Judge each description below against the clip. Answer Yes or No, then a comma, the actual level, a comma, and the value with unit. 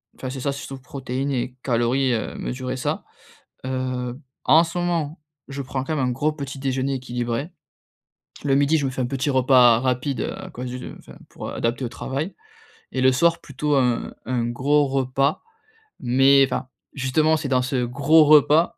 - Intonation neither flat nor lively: No, narrow, 2.1 semitones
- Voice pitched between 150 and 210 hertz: No, low, 135 Hz